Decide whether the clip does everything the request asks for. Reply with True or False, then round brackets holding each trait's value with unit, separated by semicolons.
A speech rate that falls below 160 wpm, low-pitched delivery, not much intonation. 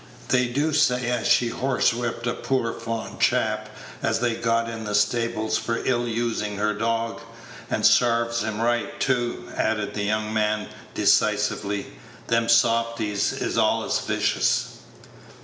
True (140 wpm; 115 Hz; 1.6 semitones)